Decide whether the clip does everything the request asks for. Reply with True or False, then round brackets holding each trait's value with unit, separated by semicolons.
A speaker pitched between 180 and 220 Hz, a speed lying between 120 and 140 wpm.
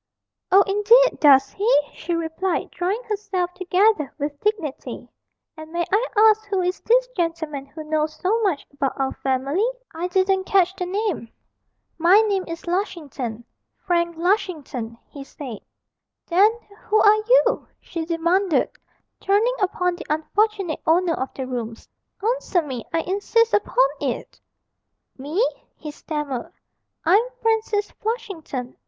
False (355 Hz; 135 wpm)